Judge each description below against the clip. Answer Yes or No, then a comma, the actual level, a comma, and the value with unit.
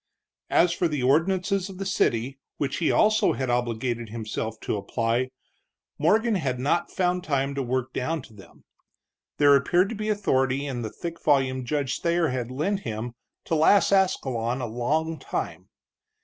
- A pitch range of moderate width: No, wide, 6.0 semitones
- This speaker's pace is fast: No, average, 165 wpm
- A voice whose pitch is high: No, medium, 140 Hz